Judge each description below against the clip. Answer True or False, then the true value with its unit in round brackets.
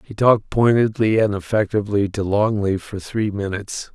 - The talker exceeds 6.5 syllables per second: False (5.2 syllables/s)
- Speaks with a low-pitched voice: True (105 Hz)